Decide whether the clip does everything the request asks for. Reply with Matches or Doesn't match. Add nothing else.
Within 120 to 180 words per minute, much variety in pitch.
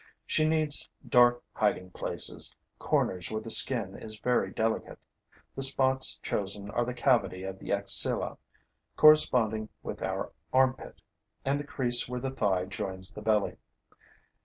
Doesn't match